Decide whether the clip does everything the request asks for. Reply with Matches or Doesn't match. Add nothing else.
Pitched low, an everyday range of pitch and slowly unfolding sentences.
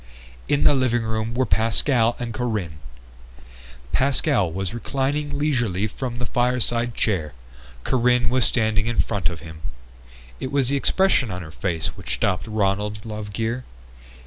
Doesn't match